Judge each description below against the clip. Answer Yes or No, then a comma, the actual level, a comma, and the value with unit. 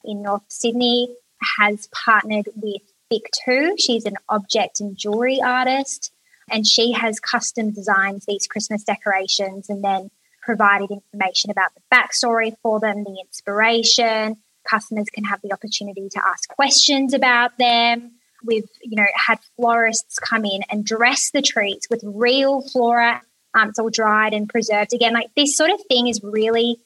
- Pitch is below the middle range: No, high, 225 Hz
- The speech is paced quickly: No, average, 155 wpm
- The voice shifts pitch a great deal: No, average, 2.7 semitones